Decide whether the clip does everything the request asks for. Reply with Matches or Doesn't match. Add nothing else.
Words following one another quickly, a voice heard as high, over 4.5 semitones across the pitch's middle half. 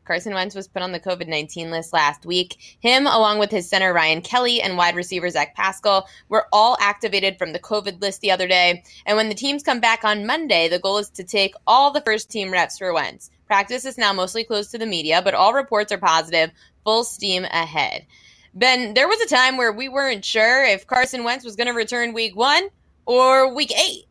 Matches